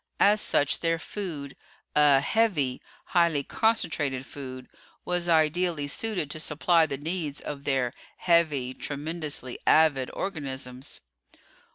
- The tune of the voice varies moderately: Yes, average, 3.7 semitones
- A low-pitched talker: No, medium, 150 Hz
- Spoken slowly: Yes, slow, 110 wpm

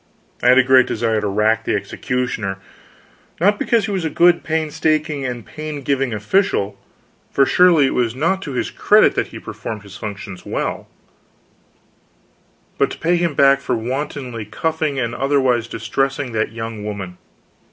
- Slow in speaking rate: No, average, 160 wpm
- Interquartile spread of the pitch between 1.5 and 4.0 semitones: No, wide, 5.6 semitones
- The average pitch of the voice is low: Yes, low, 130 Hz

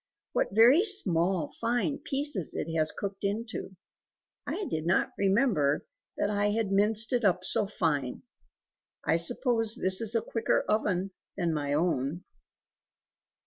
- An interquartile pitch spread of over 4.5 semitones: Yes, average, 5.3 semitones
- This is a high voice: Yes, high, 200 Hz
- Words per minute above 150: No, average, 140 wpm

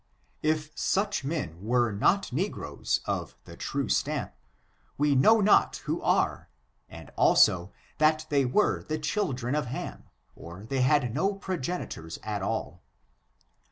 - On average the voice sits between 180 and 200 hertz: No, medium, 140 Hz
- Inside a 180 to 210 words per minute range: No, slow, 135 wpm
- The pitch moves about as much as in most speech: No, wide, 6.2 semitones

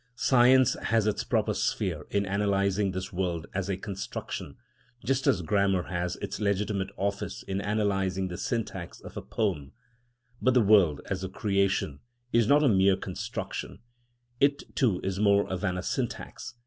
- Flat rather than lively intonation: Yes, narrow, 2.3 semitones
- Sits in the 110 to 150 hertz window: No, low, 100 Hz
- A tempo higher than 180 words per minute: No, average, 160 wpm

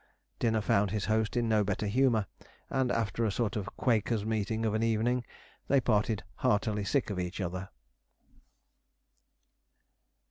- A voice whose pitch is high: No, low, 110 Hz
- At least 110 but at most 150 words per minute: Yes, average, 145 wpm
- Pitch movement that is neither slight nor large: No, narrow, 2.1 semitones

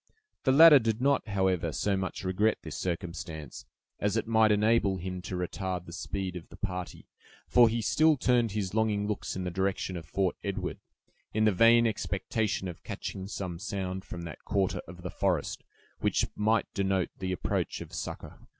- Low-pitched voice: Yes, very low, 95 Hz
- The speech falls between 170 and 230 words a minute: Yes, average, 180 wpm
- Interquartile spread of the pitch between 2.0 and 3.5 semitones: Yes, average, 3.2 semitones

